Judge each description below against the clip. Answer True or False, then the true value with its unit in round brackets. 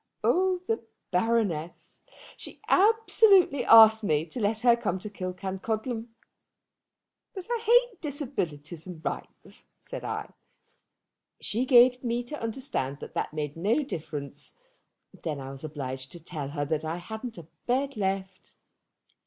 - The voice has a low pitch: False (210 Hz)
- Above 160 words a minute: False (135 wpm)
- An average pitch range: False (8.0 semitones)